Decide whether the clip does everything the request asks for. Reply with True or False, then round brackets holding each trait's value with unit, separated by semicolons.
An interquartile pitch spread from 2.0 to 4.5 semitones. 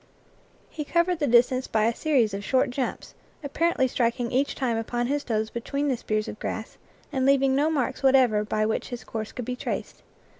True (3.4 semitones)